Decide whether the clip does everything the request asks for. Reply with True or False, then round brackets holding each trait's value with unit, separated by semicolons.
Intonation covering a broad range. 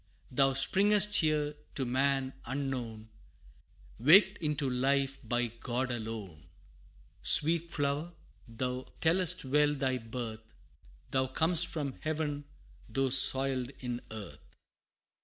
False (3.5 semitones)